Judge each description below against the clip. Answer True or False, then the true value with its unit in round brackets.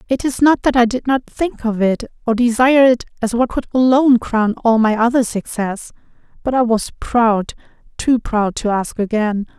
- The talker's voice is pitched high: True (235 Hz)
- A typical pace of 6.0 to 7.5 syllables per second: False (4.8 syllables/s)